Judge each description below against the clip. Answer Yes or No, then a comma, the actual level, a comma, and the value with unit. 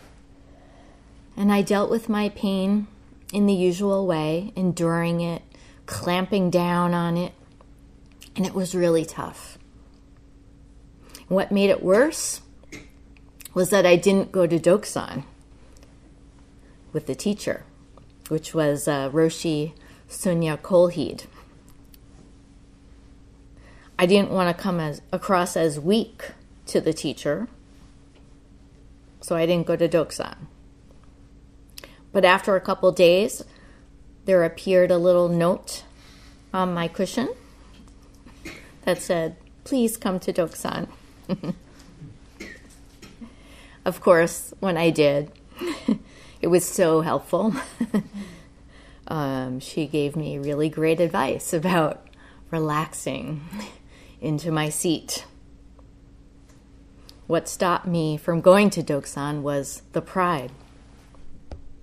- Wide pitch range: No, average, 3.8 semitones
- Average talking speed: No, slow, 105 wpm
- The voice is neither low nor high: Yes, medium, 170 Hz